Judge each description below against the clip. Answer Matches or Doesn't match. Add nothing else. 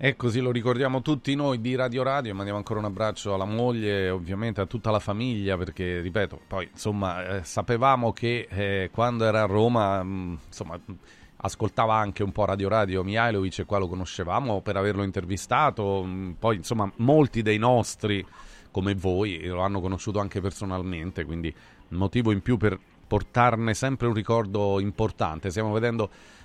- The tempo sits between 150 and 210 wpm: Matches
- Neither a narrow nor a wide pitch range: Matches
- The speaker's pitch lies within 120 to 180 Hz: Doesn't match